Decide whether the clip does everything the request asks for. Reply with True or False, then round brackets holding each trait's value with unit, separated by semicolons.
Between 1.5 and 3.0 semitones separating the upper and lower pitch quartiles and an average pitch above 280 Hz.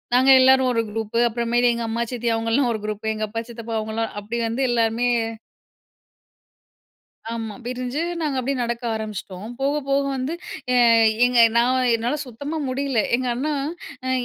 False (2.4 semitones; 240 Hz)